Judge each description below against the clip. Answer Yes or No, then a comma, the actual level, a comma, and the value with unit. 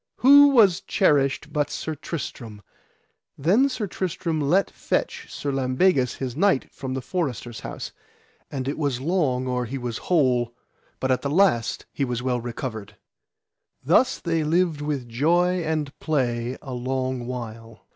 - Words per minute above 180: No, average, 150 wpm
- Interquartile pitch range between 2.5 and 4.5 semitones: No, average, 5.1 semitones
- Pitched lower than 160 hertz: Yes, low, 135 Hz